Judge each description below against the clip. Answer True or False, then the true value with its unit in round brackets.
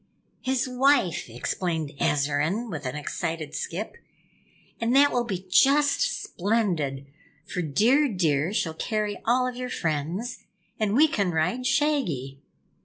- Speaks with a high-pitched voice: True (200 Hz)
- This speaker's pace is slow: True (130 wpm)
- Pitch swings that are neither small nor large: False (8.1 semitones)